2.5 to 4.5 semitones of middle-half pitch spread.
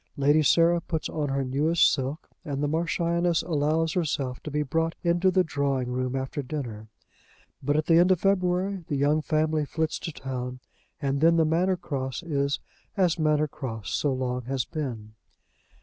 Yes: average, 3.6 semitones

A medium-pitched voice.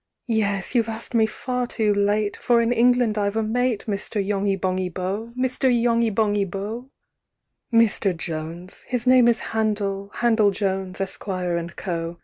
No: high, 210 Hz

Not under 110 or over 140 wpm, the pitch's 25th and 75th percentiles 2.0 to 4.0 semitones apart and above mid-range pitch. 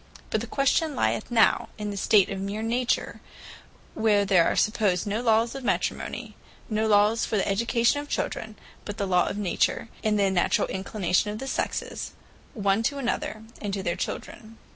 No: average, 185 wpm; narrow, 2.6 semitones; high, 215 Hz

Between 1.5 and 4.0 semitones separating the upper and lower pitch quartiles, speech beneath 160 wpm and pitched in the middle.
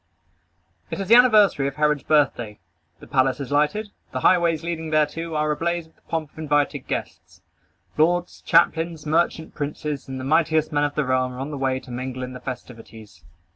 No: average, 3.7 semitones; average, 190 wpm; medium, 150 Hz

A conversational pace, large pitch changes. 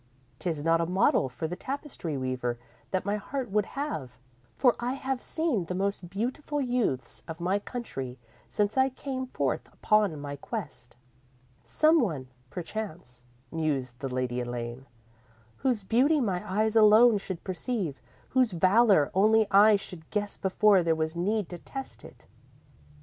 Yes: average, 150 wpm; wide, 7.9 semitones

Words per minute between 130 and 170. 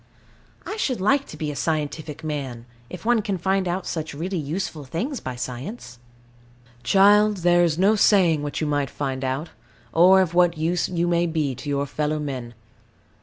No: average, 180 wpm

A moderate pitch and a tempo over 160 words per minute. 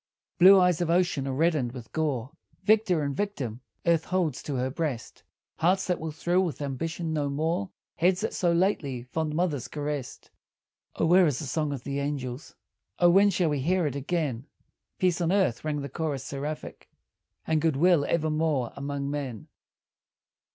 Yes: medium, 155 Hz; average, 170 wpm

